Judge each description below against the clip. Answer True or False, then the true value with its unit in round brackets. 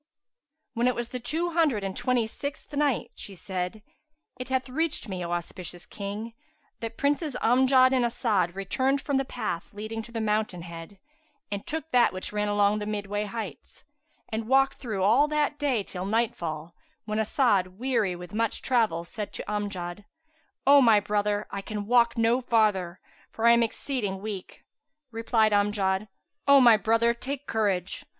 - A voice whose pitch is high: True (220 Hz)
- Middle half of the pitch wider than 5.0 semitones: False (4.1 semitones)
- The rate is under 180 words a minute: True (170 wpm)